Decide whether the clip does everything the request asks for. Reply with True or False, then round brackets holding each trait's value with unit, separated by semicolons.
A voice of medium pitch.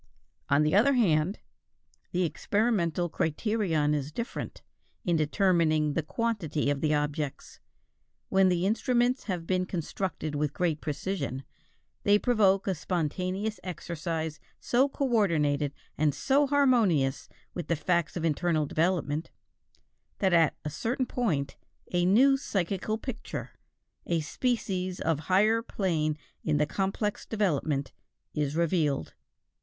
True (175 Hz)